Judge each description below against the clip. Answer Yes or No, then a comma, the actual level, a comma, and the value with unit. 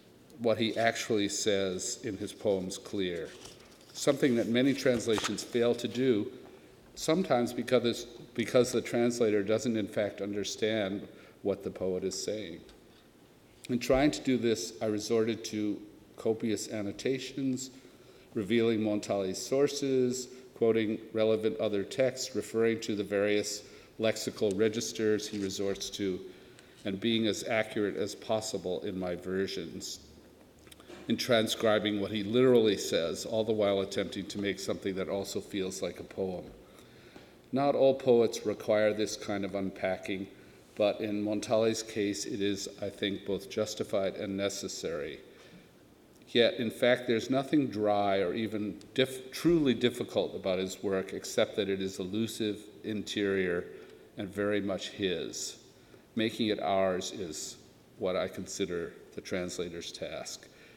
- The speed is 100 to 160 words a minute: Yes, slow, 135 wpm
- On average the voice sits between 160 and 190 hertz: No, low, 110 Hz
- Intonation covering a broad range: No, average, 3.1 semitones